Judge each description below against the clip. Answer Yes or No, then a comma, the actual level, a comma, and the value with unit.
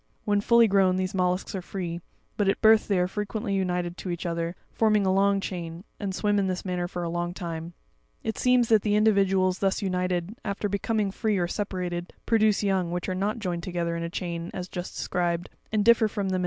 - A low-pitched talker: No, high, 190 Hz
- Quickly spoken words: Yes, fast, 220 wpm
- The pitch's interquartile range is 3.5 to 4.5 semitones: No, average, 2.7 semitones